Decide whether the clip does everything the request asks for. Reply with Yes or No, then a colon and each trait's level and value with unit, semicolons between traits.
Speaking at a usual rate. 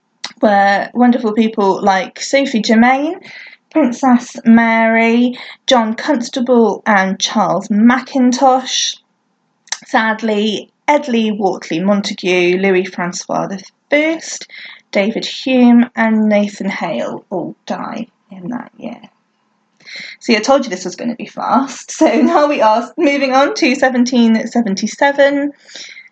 No: slow, 110 wpm